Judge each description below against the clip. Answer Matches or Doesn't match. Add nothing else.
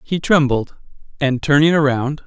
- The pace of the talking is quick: Doesn't match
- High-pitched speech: Doesn't match